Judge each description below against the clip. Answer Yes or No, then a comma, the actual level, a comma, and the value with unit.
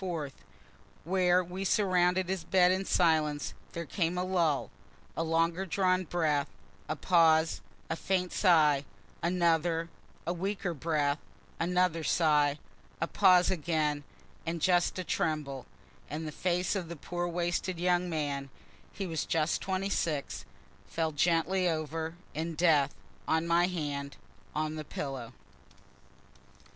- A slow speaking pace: Yes, slow, 130 wpm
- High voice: No, medium, 165 Hz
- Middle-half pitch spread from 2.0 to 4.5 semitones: Yes, narrow, 2.6 semitones